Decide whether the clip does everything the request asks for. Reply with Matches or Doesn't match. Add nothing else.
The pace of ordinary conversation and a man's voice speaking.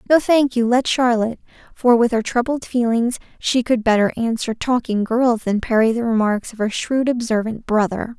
Doesn't match